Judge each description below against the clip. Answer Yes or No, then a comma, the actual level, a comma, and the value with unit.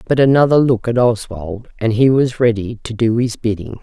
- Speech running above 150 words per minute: Yes, fast, 205 wpm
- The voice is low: Yes, low, 115 Hz